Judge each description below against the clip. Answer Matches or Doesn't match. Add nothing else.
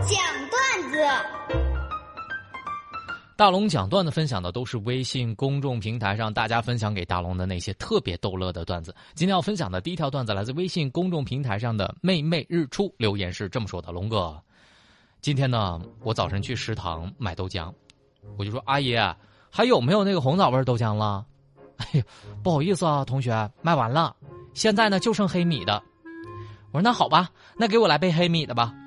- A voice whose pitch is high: Doesn't match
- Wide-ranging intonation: Matches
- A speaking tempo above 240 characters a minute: Matches